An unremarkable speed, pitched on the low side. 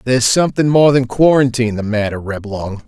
Yes: average, 165 wpm; low, 120 Hz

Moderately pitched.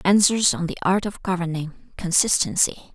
Yes: medium, 180 Hz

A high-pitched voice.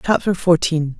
No: medium, 165 Hz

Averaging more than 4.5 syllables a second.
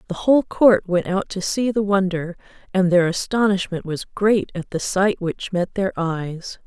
No: 4.4 syllables/s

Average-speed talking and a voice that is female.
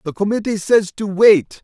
No: average, 185 wpm; male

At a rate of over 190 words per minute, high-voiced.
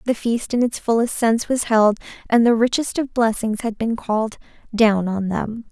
Yes: average, 200 wpm; high, 225 Hz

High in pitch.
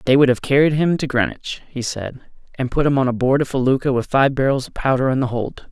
No: low, 135 Hz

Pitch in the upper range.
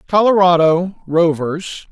No: medium, 175 Hz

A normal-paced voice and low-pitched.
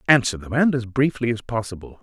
No: fast, 210 wpm; low, 120 Hz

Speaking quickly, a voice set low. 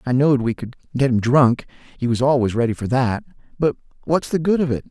Yes: fast, 210 wpm; low, 130 Hz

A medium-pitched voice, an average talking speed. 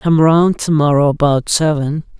Yes: medium, 150 Hz; average, 165 wpm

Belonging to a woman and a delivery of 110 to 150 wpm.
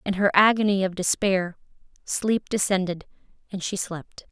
Yes: female; average, 140 wpm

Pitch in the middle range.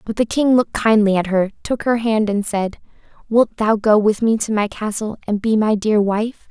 No: high, 215 Hz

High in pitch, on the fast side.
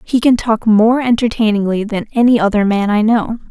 No: high, 220 Hz; average, 190 wpm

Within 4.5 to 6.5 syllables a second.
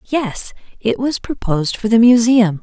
Yes: 4.6 syllables/s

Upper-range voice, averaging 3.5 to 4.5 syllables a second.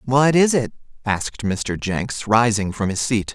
No: low, 115 Hz; 4.1 syllables/s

